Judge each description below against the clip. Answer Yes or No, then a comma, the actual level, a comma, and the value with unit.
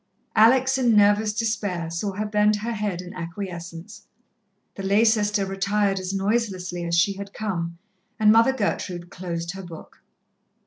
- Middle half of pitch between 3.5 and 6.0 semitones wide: No, average, 3.0 semitones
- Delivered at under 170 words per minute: Yes, average, 150 wpm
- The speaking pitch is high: Yes, high, 200 Hz